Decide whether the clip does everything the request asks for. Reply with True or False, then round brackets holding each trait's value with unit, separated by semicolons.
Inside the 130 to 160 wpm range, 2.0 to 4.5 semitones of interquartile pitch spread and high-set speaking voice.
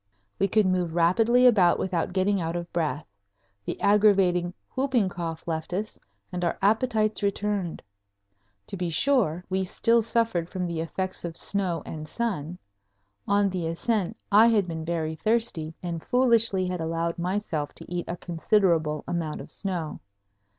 False (155 wpm; 3.9 semitones; 180 Hz)